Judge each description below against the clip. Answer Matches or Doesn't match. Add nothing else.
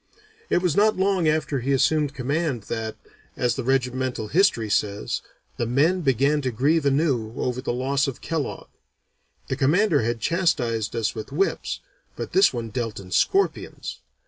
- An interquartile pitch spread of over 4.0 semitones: Matches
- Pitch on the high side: Doesn't match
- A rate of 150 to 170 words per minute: Matches